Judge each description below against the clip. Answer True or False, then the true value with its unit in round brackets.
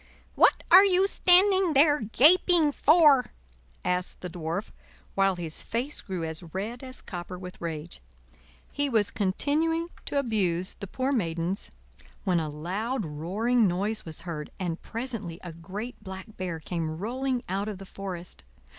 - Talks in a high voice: True (195 Hz)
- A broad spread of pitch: True (7.0 semitones)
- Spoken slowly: False (150 wpm)